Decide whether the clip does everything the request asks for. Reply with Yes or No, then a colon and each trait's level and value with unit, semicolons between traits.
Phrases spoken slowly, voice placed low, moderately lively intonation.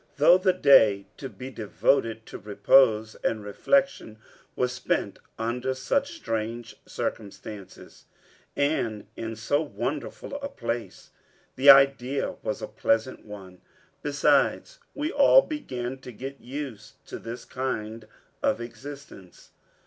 Yes: slow, 120 wpm; low, 125 Hz; average, 4.4 semitones